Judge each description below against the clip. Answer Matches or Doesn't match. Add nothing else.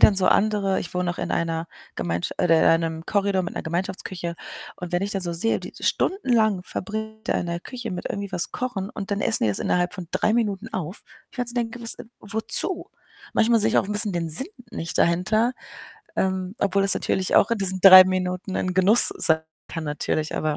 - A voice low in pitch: Doesn't match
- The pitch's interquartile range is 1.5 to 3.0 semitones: Doesn't match